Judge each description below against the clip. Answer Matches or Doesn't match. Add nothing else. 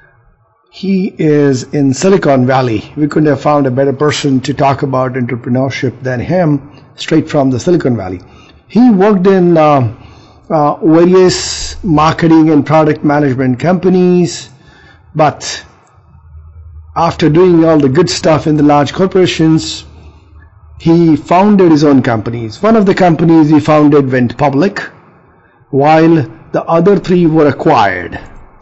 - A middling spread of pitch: Matches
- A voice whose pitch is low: Doesn't match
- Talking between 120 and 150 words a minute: Matches